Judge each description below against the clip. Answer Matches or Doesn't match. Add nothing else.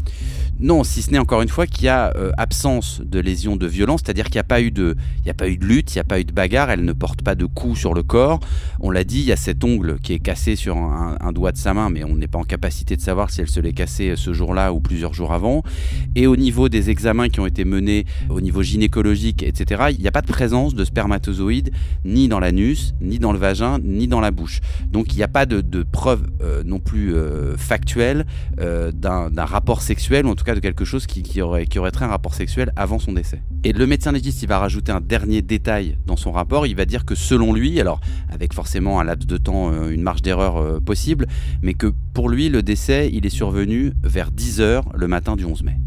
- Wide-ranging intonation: Doesn't match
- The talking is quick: Matches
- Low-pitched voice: Matches